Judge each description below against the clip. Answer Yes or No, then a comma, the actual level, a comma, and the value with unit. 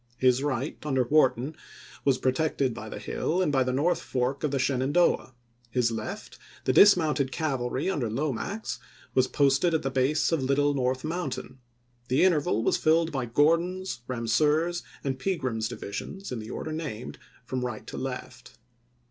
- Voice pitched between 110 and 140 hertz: Yes, low, 135 Hz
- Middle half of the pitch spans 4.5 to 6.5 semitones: No, average, 3.8 semitones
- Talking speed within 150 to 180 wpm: Yes, average, 165 wpm